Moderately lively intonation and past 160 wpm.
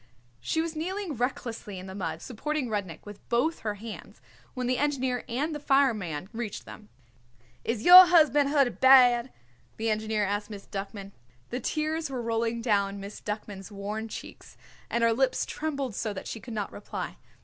Yes: average, 4.9 semitones; average, 170 wpm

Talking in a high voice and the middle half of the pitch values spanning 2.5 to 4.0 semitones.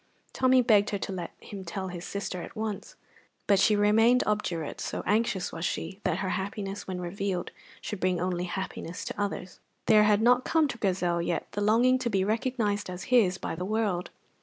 Yes: high, 200 Hz; average, 3.1 semitones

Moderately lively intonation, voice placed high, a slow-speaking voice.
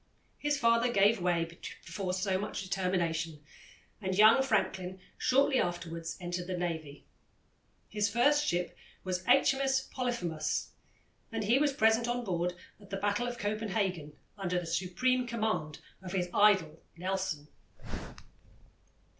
Yes: average, 4.8 semitones; high, 195 Hz; slow, 130 wpm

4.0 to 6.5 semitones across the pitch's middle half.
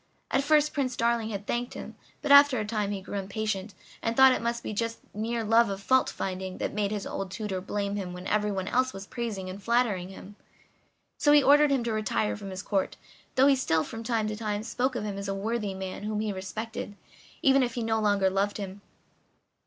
No: average, 3.2 semitones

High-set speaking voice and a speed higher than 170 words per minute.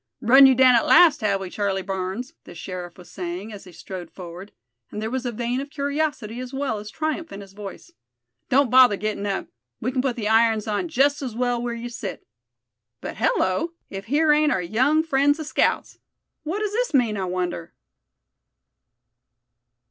Yes: high, 235 Hz; average, 190 wpm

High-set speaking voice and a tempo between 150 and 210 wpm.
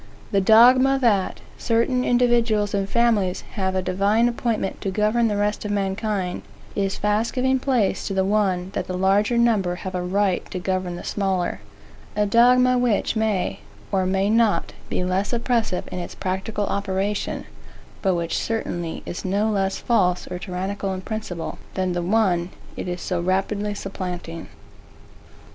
Yes: high, 200 Hz; average, 160 wpm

